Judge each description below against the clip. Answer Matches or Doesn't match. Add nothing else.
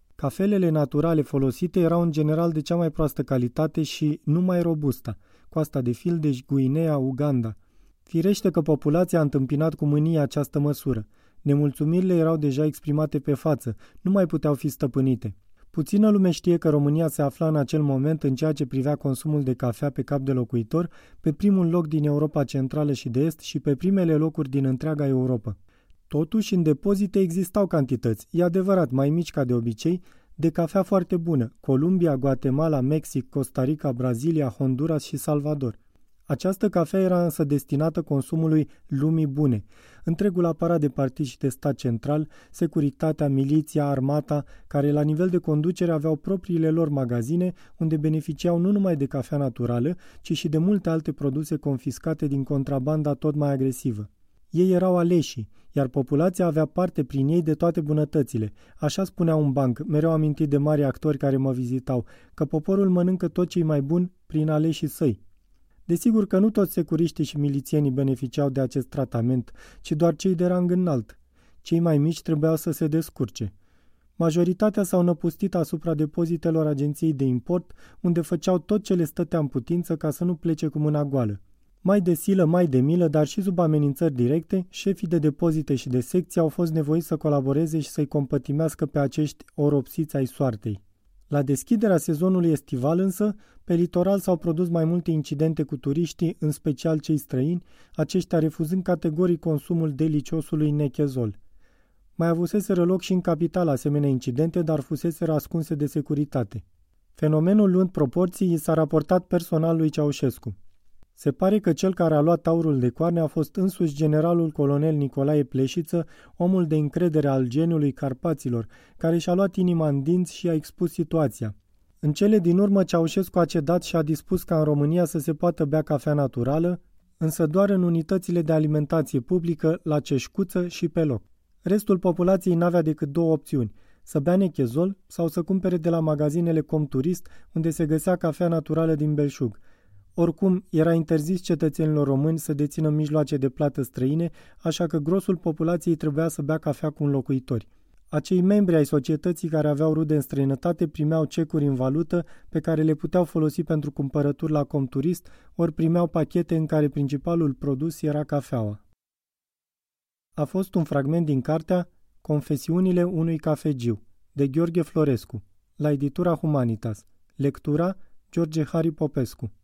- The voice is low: Doesn't match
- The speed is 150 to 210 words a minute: Matches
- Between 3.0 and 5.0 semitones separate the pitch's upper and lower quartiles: Matches